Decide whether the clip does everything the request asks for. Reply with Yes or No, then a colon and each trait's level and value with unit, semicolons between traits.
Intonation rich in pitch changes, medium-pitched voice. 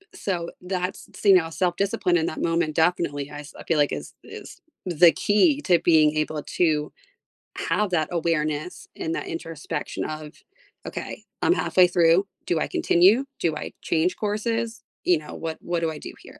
No: average, 2.8 semitones; medium, 170 Hz